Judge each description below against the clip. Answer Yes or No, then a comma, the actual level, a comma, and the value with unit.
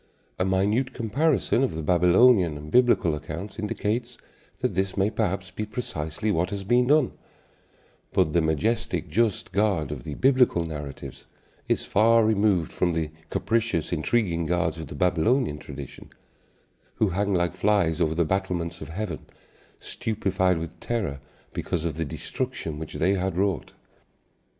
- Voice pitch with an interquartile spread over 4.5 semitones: Yes, average, 5.1 semitones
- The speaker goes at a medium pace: Yes, average, 150 wpm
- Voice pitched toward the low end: Yes, very low, 95 Hz